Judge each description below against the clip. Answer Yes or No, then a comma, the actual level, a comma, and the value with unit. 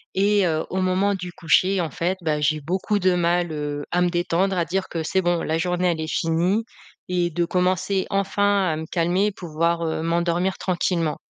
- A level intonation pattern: Yes, narrow, 2.3 semitones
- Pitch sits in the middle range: Yes, medium, 175 Hz